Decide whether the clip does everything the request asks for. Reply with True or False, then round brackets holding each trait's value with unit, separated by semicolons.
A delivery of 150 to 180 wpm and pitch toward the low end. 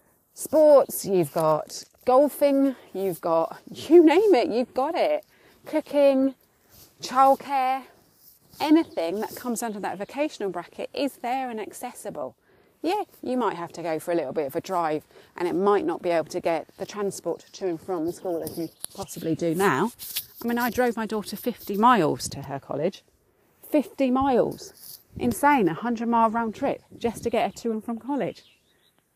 False (175 wpm; 235 Hz)